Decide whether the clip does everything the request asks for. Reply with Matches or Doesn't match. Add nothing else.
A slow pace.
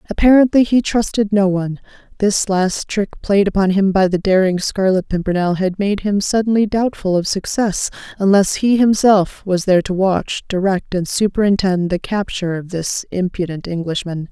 Doesn't match